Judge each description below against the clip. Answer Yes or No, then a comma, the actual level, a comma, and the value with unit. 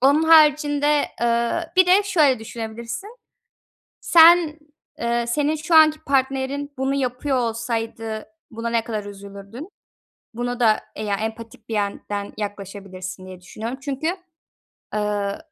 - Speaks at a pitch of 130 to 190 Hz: No, high, 235 Hz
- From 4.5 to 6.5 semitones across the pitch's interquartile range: Yes, average, 5.3 semitones